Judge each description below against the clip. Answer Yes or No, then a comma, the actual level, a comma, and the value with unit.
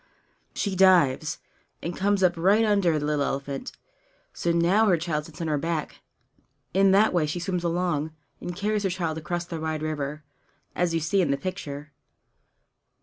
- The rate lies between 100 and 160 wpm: No, average, 175 wpm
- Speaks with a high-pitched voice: No, medium, 170 Hz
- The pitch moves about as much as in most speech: Yes, average, 3.5 semitones